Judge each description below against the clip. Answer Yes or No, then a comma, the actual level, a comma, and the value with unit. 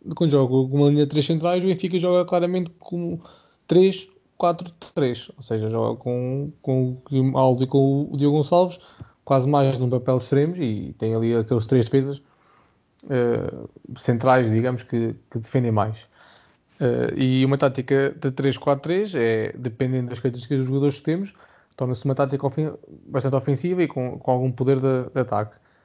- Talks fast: No, average, 175 wpm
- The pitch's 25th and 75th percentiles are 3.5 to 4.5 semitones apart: No, average, 2.8 semitones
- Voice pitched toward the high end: No, low, 135 Hz